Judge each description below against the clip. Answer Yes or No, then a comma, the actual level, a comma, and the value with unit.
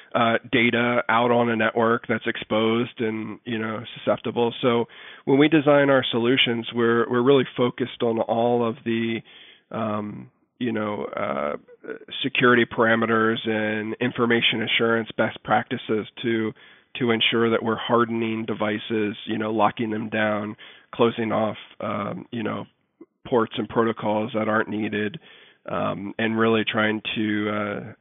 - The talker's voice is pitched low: Yes, low, 115 Hz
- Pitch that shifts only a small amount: Yes, narrow, 1.6 semitones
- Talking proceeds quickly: No, average, 140 wpm